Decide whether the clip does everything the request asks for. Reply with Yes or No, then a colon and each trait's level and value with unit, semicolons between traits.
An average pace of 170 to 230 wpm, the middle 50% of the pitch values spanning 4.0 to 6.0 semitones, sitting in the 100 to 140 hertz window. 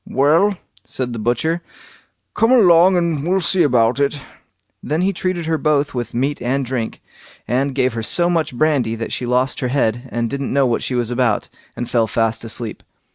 Yes: average, 190 wpm; average, 5.2 semitones; low, 135 Hz